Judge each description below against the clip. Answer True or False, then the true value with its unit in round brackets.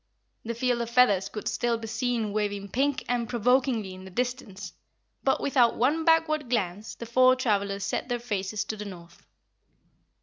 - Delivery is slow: False (170 wpm)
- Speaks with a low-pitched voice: False (235 Hz)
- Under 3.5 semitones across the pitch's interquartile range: False (3.8 semitones)